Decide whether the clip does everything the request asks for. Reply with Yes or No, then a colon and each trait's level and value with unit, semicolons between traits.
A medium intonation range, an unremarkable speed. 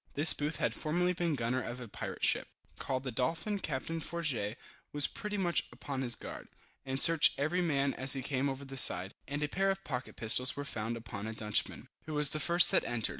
No: average, 4.6 semitones; fast, 220 wpm